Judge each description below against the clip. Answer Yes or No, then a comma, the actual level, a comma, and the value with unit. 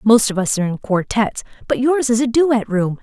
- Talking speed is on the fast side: Yes, fast, 240 wpm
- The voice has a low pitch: No, high, 225 Hz